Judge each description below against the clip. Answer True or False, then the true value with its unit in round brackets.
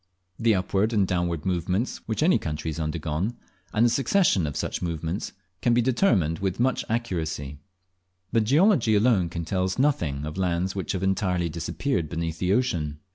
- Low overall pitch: True (95 Hz)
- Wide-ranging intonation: True (5.7 semitones)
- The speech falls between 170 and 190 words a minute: True (175 wpm)